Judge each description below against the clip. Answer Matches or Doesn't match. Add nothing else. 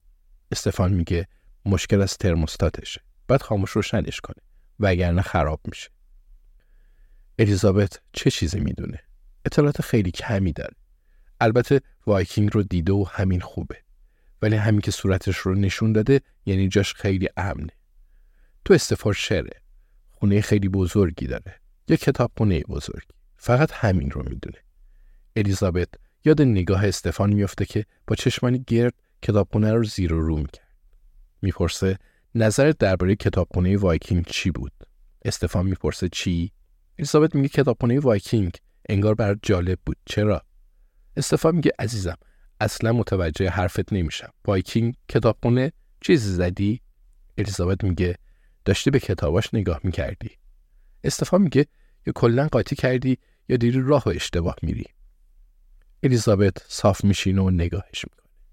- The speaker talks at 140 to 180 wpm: Doesn't match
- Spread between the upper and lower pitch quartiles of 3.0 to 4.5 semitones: Matches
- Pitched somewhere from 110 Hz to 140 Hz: Doesn't match